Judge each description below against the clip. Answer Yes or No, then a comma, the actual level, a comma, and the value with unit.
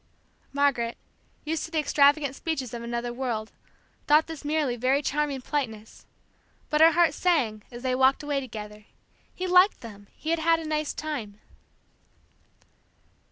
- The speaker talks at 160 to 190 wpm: No, average, 150 wpm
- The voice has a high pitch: Yes, very high, 280 Hz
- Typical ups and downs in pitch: Yes, average, 4.5 semitones